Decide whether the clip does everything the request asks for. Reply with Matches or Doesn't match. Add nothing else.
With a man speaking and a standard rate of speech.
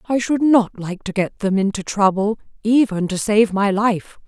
Doesn't match